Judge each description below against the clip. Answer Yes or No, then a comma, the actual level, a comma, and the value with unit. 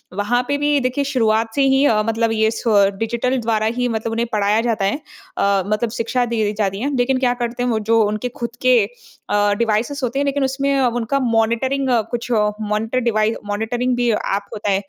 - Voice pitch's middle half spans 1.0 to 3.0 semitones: Yes, average, 2.7 semitones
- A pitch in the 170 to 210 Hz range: No, high, 230 Hz